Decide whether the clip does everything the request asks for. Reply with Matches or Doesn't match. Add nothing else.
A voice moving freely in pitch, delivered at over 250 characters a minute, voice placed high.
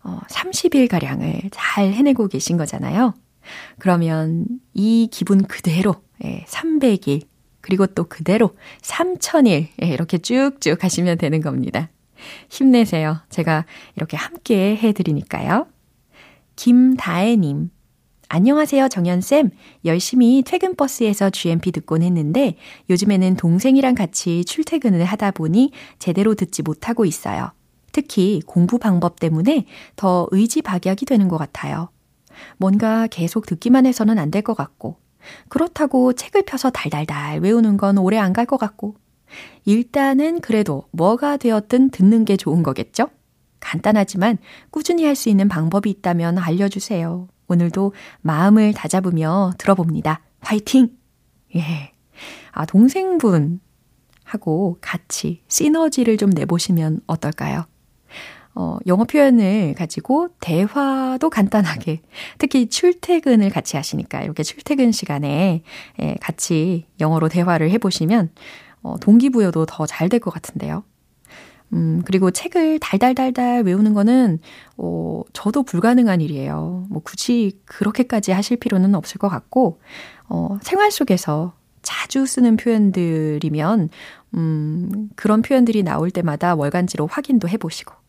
Matches